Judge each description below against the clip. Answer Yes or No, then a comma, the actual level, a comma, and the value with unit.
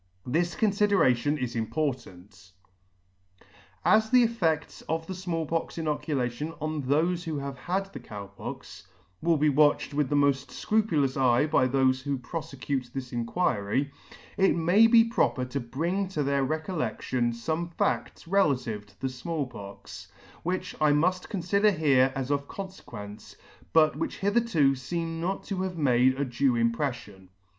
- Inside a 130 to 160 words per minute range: Yes, average, 150 wpm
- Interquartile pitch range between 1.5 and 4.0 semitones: No, average, 5.2 semitones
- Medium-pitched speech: Yes, medium, 145 Hz